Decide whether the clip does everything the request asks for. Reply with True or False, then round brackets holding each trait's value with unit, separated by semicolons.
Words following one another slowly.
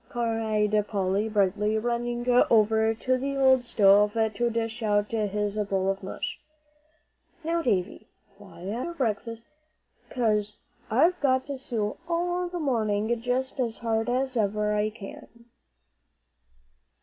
True (130 wpm)